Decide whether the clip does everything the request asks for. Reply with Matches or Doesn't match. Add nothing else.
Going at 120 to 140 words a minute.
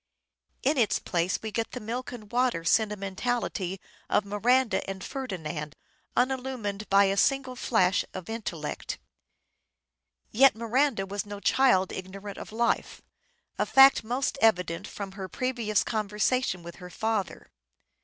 Matches